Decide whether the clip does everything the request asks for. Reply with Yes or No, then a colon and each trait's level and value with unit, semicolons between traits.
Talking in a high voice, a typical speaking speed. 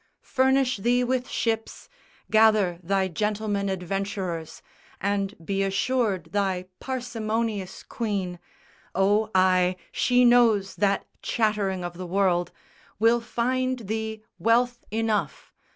No: high, 210 Hz; slow, 105 wpm